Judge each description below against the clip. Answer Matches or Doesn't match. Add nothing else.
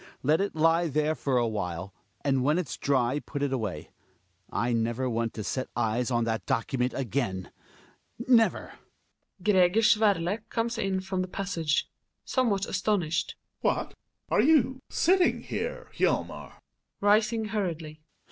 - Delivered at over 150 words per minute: Doesn't match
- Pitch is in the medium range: Matches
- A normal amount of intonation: Doesn't match